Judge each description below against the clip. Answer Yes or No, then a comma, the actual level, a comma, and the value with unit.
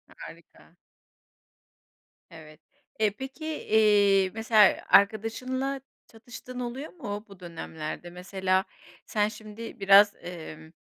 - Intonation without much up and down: No, average, 3.6 semitones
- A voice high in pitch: Yes, high, 210 Hz